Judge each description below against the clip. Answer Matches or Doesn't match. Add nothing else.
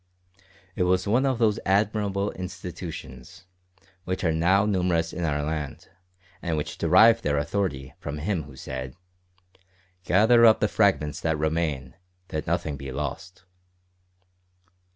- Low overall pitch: Matches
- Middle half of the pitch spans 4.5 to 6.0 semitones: Matches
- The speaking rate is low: Matches